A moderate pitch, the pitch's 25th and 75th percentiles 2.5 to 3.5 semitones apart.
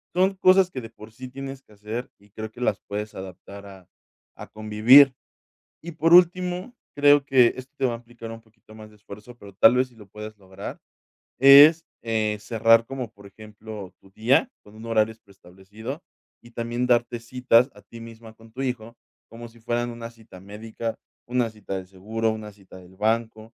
No: low, 115 Hz; average, 2.9 semitones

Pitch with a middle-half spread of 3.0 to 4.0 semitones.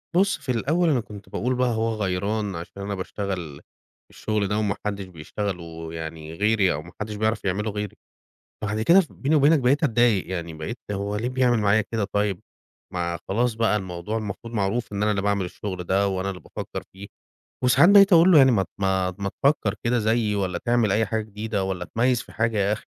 Yes: average, 3.4 semitones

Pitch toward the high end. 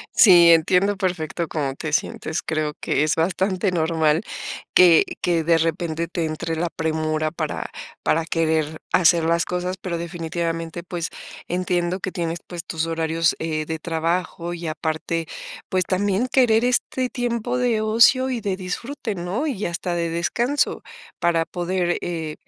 No: medium, 170 Hz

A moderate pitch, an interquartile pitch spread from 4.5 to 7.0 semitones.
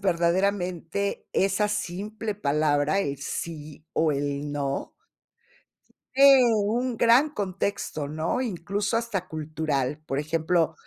Yes: medium, 175 Hz; wide, 5.4 semitones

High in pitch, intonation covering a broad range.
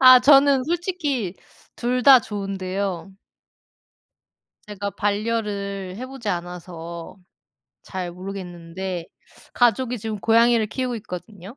No: high, 205 Hz; average, 4.9 semitones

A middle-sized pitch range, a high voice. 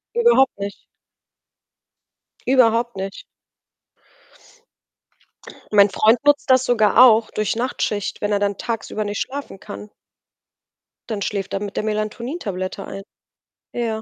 Yes: average, 3.1 semitones; high, 215 Hz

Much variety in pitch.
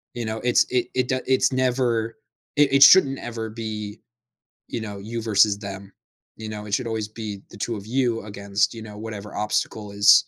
No: narrow, 2.6 semitones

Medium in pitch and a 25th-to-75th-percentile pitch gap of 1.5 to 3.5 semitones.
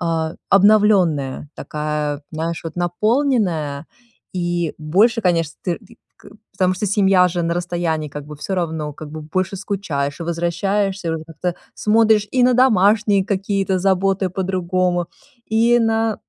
No: medium, 180 Hz; average, 3.9 semitones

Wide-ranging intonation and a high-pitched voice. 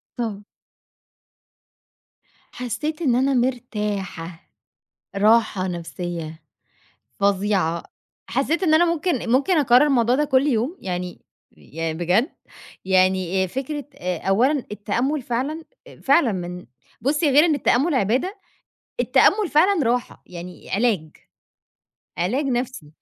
Yes: wide, 7.2 semitones; high, 240 Hz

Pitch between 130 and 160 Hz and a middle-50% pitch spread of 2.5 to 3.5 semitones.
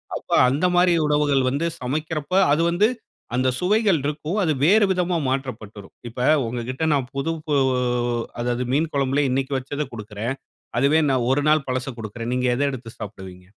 No: low, 135 Hz; average, 4.0 semitones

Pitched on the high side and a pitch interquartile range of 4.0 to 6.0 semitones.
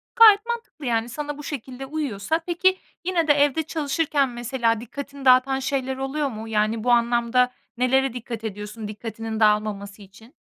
Yes: very high, 255 Hz; average, 4.4 semitones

